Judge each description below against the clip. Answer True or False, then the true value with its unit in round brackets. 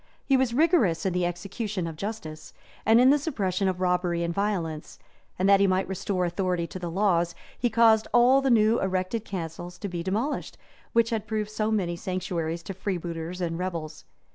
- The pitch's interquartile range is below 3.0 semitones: False (4.0 semitones)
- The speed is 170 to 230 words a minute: True (190 wpm)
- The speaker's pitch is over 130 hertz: True (185 Hz)